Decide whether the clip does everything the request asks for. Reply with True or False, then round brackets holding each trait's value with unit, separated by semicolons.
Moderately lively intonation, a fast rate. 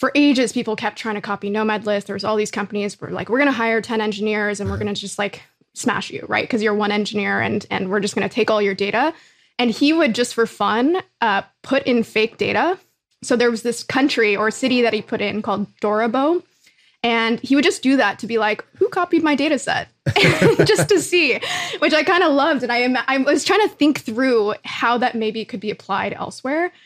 True (4.9 semitones; 230 wpm)